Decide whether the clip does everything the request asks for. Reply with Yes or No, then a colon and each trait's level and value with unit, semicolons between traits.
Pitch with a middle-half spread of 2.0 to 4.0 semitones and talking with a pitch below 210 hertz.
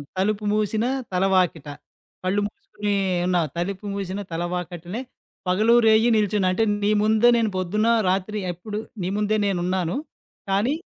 Yes: average, 2.8 semitones; high, 200 Hz